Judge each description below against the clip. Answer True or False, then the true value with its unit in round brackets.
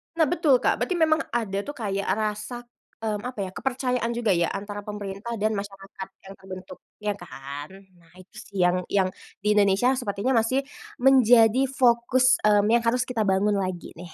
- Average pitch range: True (4.1 semitones)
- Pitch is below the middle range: False (210 Hz)